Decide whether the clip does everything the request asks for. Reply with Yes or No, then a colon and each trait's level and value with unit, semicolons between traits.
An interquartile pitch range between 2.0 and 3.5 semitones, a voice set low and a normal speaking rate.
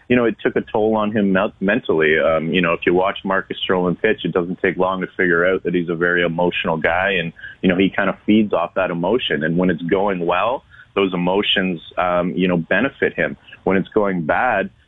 No: narrow, 2.5 semitones; very low, 90 Hz; fast, 230 wpm